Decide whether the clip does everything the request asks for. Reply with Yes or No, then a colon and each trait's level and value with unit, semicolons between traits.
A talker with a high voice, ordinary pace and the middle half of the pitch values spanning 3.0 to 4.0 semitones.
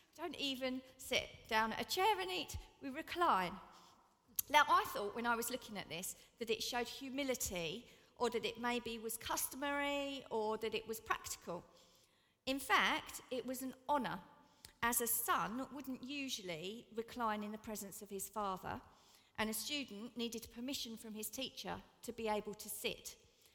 Yes: high, 235 Hz; average, 170 wpm; average, 3.6 semitones